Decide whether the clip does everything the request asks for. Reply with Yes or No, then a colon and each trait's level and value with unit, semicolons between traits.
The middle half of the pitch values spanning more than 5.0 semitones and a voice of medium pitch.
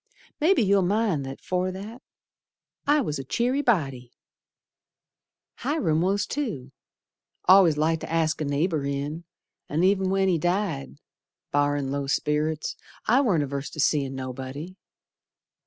Yes: wide, 5.5 semitones; medium, 160 Hz